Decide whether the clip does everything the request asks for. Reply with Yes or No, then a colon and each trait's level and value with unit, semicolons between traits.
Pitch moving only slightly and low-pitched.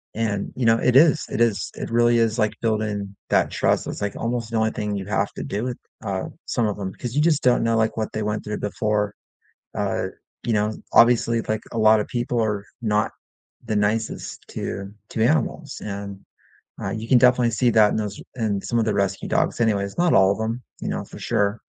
Yes: narrow, 2.2 semitones; low, 110 Hz